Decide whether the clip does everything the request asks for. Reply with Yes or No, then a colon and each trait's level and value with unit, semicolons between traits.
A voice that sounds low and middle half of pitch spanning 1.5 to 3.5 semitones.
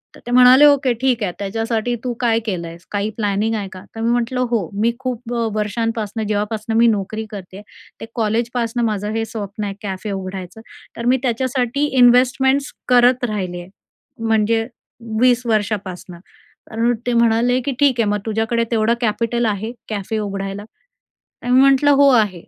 No: high, 225 Hz; average, 2.9 semitones